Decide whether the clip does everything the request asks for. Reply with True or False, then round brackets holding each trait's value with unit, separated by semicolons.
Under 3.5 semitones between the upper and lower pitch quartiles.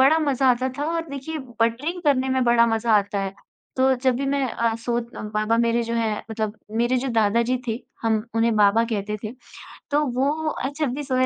True (2.8 semitones)